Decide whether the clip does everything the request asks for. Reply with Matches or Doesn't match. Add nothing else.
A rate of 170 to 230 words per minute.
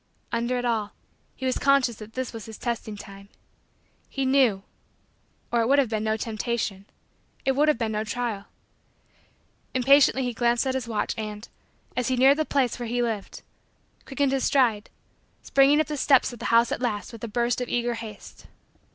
Matches